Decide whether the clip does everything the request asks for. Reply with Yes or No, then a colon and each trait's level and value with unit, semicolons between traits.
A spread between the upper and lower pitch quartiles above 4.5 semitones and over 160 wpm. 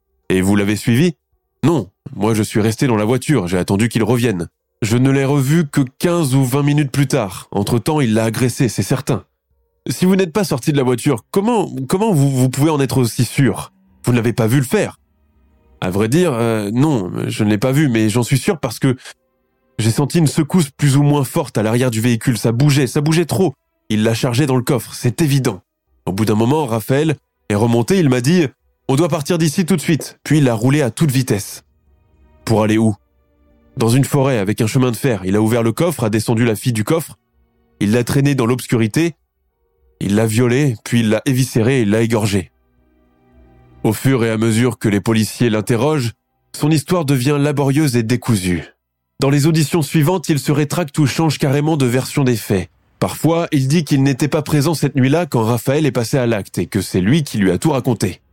Yes: average, 5.1 semitones; fast, 220 wpm